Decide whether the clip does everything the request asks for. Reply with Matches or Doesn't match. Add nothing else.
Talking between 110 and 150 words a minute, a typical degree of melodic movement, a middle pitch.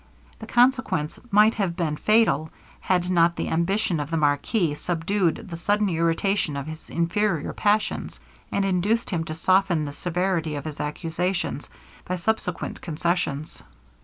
Matches